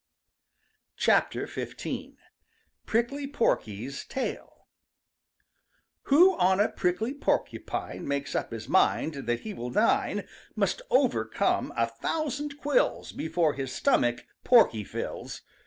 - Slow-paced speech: Yes, slow, 105 wpm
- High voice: Yes, high, 195 Hz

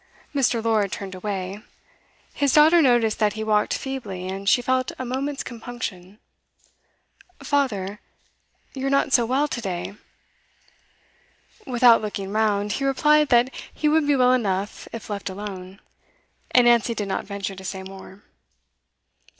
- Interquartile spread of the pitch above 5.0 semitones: No, average, 4.7 semitones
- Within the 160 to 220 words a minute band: No, average, 145 wpm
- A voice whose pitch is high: Yes, high, 220 Hz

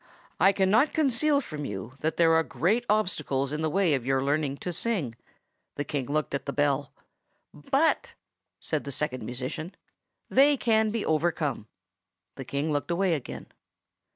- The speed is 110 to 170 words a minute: Yes, average, 160 wpm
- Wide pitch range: Yes, wide, 6.3 semitones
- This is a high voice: No, medium, 155 Hz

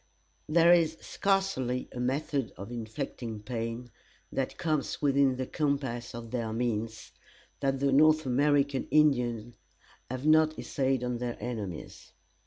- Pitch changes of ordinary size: Yes, average, 3.7 semitones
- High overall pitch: No, low, 130 Hz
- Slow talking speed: Yes, slow, 130 wpm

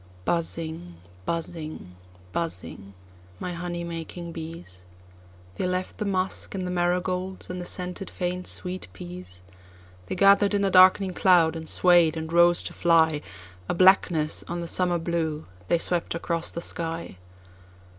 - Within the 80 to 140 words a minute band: Yes, slow, 135 wpm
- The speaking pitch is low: No, medium, 170 Hz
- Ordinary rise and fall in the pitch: Yes, average, 3.2 semitones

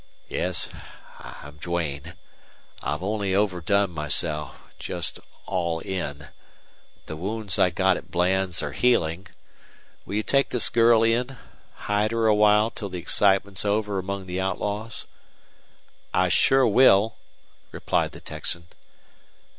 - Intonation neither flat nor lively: Yes, average, 3.5 semitones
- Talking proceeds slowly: Yes, slow, 125 wpm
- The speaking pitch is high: No, very low, 95 Hz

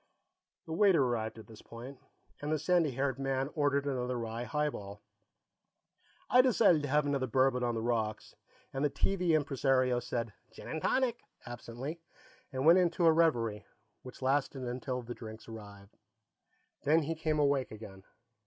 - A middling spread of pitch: Yes, average, 4.3 semitones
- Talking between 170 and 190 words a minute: No, average, 160 wpm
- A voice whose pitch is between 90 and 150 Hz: Yes, low, 135 Hz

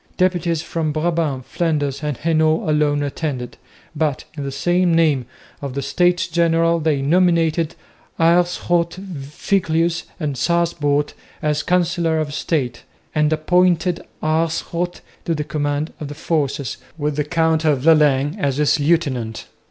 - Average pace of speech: No, slow, 130 wpm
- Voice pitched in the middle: Yes, medium, 155 Hz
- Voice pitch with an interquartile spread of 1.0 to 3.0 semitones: Yes, average, 2.7 semitones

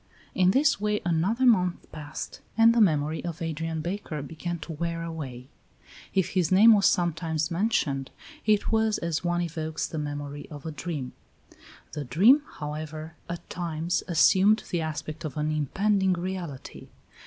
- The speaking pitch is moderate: Yes, medium, 165 Hz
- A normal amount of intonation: Yes, average, 3.5 semitones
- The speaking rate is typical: Yes, average, 155 wpm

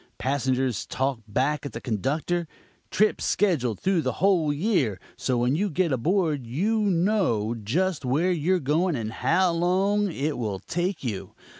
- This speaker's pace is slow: No, average, 155 wpm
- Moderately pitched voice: Yes, medium, 155 Hz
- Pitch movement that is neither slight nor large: No, wide, 6.6 semitones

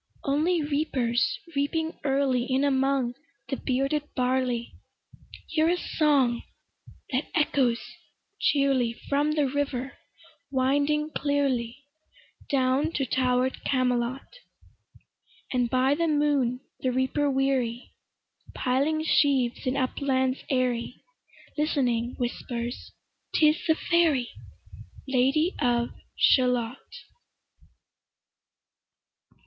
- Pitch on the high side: Yes, very high, 270 Hz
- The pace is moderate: No, slow, 90 wpm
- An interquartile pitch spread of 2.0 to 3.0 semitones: Yes, narrow, 2.6 semitones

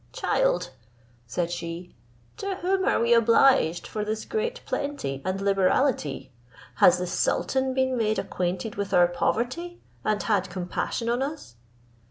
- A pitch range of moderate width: No, wide, 7.0 semitones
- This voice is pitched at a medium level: No, high, 215 Hz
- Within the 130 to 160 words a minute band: Yes, average, 140 wpm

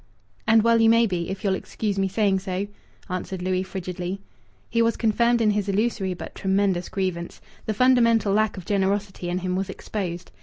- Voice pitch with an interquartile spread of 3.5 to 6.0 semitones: No, average, 2.8 semitones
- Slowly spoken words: No, average, 185 wpm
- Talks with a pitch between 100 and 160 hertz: No, high, 195 Hz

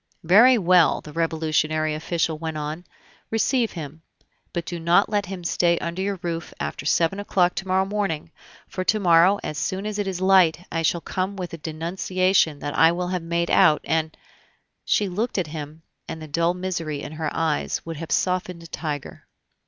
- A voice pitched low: No, medium, 170 Hz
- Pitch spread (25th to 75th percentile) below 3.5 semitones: Yes, average, 2.8 semitones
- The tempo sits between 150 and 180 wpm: No, average, 190 wpm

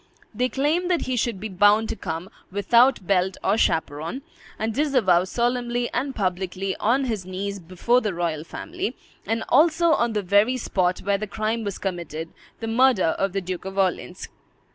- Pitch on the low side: No, high, 205 Hz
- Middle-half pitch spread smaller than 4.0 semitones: No, average, 4.8 semitones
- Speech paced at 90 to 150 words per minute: No, average, 175 wpm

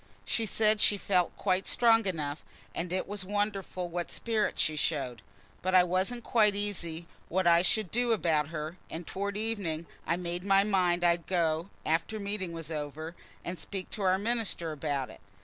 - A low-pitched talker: No, medium, 185 Hz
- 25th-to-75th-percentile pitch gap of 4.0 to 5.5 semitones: No, average, 3.6 semitones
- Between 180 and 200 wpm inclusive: Yes, average, 185 wpm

